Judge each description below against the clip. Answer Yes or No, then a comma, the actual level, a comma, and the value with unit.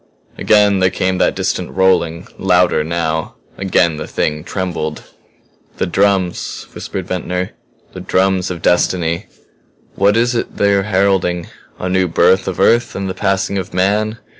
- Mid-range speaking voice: No, very low, 95 Hz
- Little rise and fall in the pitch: Yes, narrow, 1.9 semitones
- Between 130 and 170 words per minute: Yes, average, 150 wpm